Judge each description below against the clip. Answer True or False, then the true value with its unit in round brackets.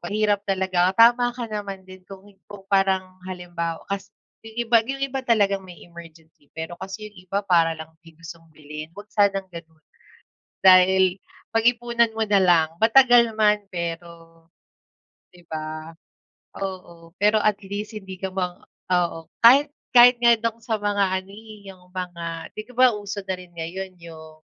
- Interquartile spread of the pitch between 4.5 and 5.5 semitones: False (3.9 semitones)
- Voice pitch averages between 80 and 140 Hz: False (190 Hz)